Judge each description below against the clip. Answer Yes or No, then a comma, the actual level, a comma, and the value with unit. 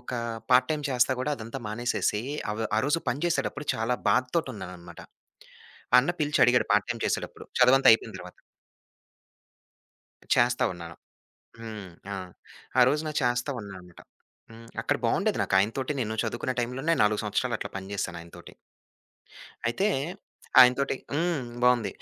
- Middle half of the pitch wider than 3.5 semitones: Yes, average, 4.2 semitones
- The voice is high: No, low, 120 Hz